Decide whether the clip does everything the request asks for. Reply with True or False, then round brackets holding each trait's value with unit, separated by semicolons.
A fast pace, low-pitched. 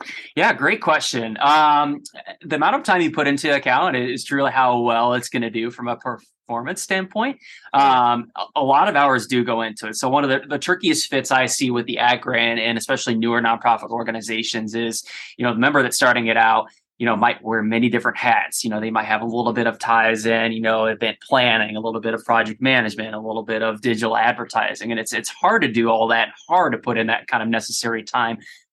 True (235 wpm; 115 Hz)